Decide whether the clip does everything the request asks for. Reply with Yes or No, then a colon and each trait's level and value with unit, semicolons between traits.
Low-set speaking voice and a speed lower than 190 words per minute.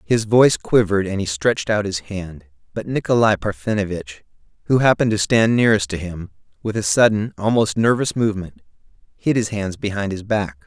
Yes: low, 105 Hz; average, 175 wpm